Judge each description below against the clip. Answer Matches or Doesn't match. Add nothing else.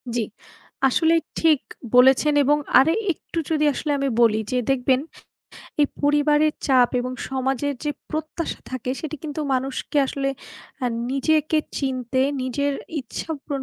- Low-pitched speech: Doesn't match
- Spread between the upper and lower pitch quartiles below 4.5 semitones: Matches